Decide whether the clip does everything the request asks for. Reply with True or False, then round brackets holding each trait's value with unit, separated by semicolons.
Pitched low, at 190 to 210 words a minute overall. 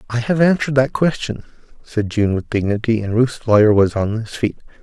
True (115 Hz; 200 wpm)